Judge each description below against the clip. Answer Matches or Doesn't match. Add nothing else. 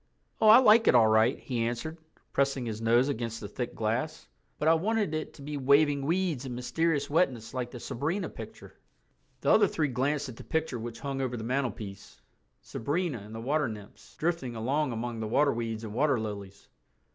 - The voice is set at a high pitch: Doesn't match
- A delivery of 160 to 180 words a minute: Doesn't match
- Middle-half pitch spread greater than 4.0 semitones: Matches